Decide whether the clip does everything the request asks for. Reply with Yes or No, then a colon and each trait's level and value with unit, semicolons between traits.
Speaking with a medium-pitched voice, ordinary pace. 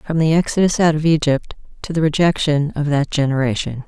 Yes: medium, 150 Hz; average, 185 wpm